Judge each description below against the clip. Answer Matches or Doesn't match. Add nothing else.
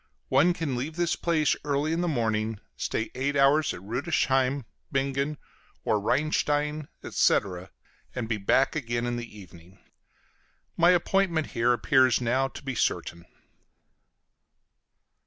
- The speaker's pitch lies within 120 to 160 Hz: Matches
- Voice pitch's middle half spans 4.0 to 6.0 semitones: Matches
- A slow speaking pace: Matches